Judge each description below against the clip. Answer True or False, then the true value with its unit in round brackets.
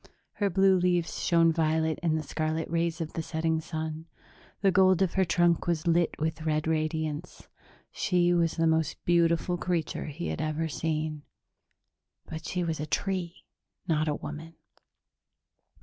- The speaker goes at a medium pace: True (160 wpm)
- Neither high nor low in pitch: True (165 Hz)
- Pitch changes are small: True (1.7 semitones)